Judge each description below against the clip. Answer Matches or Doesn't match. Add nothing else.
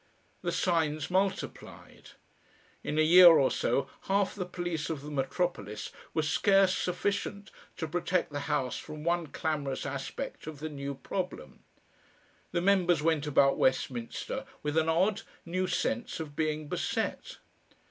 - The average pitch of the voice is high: Doesn't match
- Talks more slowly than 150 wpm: Matches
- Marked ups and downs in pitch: Doesn't match